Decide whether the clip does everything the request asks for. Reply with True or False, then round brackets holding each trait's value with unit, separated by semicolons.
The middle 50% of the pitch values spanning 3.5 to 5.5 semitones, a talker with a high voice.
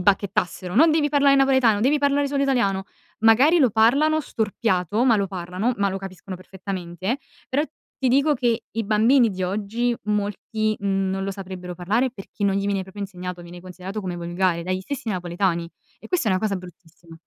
True (4.7 semitones; 200 Hz)